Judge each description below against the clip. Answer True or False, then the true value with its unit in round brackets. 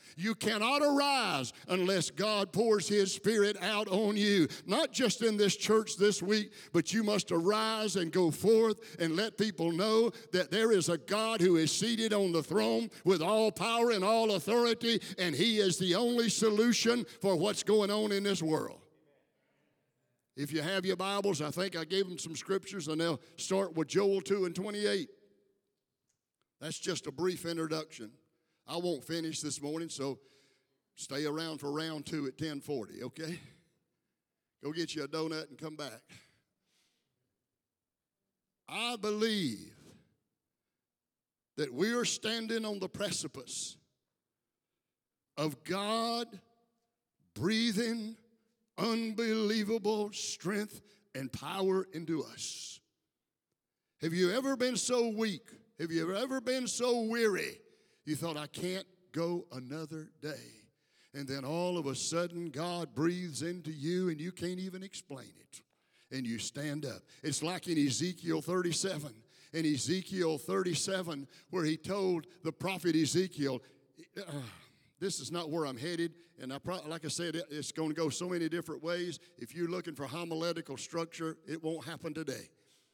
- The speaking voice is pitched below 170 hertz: False (175 Hz)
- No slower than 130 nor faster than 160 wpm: True (150 wpm)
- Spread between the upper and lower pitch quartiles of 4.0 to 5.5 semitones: True (4.7 semitones)